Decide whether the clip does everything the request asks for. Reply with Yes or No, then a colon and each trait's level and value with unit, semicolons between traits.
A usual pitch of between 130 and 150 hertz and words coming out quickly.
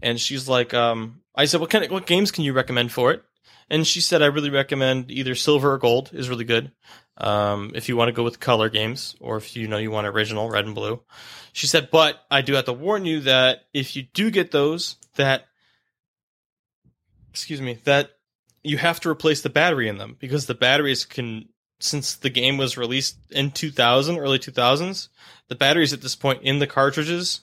Yes: low, 135 Hz; fast, 210 wpm